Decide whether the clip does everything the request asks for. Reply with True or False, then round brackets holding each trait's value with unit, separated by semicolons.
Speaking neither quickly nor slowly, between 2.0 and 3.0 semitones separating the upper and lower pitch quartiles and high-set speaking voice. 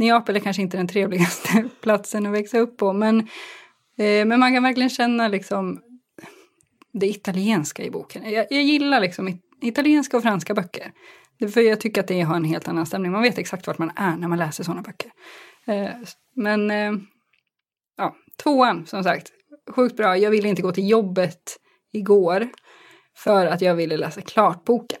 False (180 wpm; 4.1 semitones; 210 Hz)